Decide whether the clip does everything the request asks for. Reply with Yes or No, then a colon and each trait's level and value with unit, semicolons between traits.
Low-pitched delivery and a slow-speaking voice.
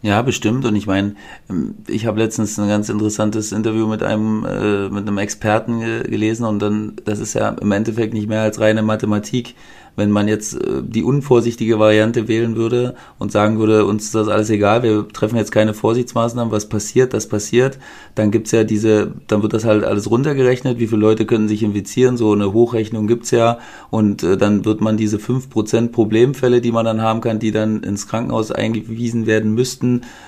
No: low, 110 Hz; fast, 190 wpm